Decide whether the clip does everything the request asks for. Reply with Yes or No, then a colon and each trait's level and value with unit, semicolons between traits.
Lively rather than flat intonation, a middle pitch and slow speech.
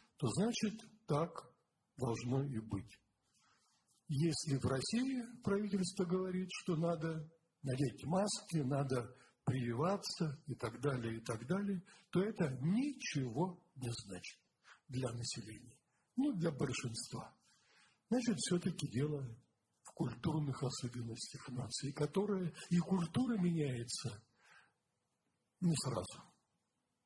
Yes: wide, 6.8 semitones; medium, 150 Hz; slow, 100 wpm